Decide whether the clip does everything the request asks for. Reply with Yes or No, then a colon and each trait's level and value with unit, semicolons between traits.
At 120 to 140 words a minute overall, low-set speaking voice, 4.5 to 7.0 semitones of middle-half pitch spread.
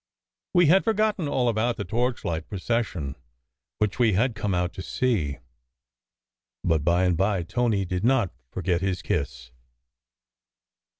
Yes: slow, 135 wpm; low, 100 Hz; wide, 5.6 semitones